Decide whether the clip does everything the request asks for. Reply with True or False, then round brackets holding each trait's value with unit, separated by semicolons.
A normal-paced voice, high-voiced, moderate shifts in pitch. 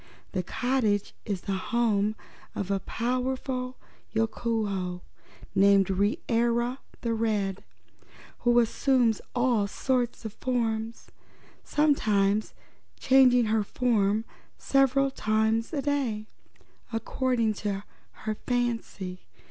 False (100 wpm; 225 Hz; 3.5 semitones)